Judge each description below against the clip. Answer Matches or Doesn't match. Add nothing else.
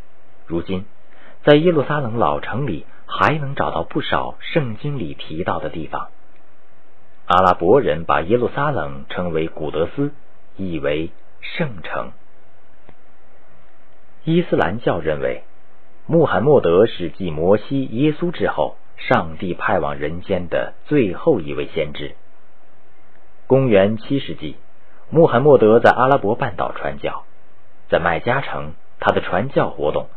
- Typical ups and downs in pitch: Doesn't match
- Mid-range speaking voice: Doesn't match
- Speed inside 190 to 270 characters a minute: Matches